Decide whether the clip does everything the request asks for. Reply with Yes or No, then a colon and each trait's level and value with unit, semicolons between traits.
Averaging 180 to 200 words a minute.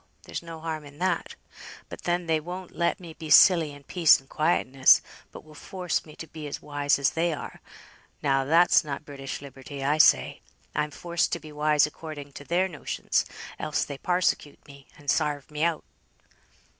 Yes: average, 185 wpm